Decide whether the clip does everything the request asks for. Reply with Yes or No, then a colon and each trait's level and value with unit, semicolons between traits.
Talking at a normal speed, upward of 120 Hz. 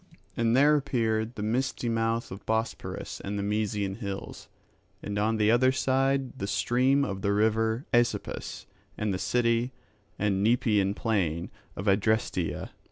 No: average, 145 wpm; low, 110 Hz